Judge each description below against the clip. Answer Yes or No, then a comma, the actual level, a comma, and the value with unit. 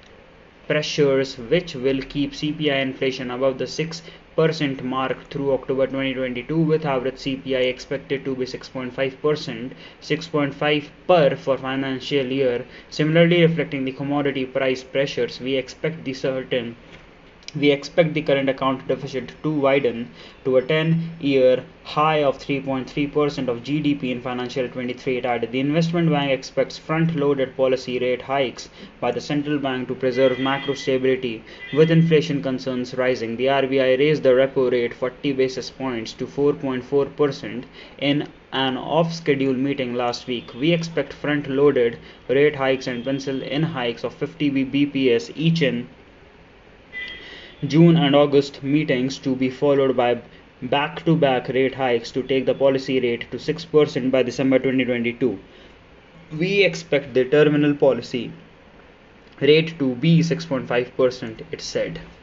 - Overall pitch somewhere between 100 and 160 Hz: Yes, low, 135 Hz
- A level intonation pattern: Yes, narrow, 2.2 semitones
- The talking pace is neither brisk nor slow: Yes, average, 150 wpm